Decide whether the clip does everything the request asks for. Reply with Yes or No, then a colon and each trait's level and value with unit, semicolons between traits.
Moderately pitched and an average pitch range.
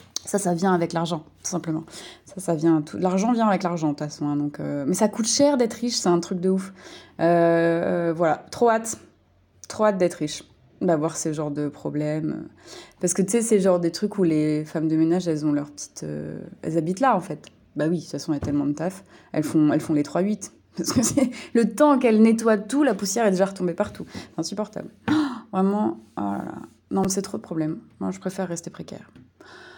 Yes: medium, 175 Hz; average, 5.0 semitones